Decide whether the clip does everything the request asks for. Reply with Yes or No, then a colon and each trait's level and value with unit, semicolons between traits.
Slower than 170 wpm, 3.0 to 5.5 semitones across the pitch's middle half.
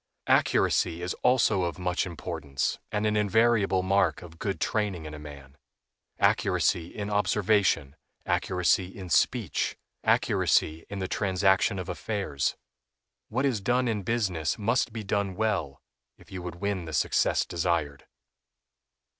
Yes: slow, 135 wpm; average, 3.9 semitones